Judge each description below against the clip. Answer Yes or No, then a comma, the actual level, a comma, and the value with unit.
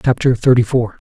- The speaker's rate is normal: Yes, average, 170 wpm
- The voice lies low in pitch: Yes, low, 120 Hz